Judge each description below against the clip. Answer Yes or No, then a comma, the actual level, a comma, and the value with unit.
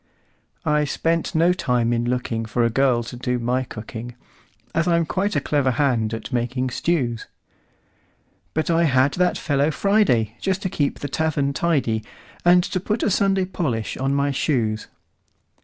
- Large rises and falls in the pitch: Yes, wide, 5.8 semitones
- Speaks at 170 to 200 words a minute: No, average, 145 wpm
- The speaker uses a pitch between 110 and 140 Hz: Yes, low, 135 Hz